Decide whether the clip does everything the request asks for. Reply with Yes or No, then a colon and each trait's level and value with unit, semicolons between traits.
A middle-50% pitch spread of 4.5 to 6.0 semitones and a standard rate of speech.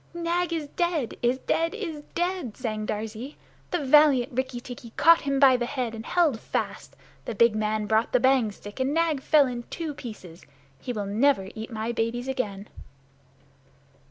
Yes: average, 5.1 semitones; average, 175 wpm